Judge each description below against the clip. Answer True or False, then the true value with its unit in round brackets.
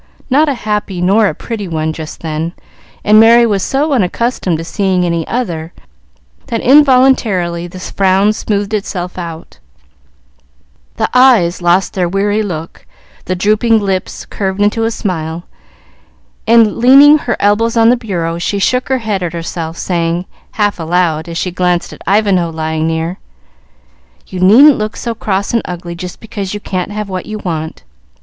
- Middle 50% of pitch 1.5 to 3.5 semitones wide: False (4.4 semitones)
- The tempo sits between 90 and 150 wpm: False (160 wpm)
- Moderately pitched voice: False (195 Hz)